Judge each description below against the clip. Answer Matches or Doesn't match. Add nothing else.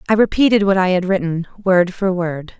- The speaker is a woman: Matches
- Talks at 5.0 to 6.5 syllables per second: Matches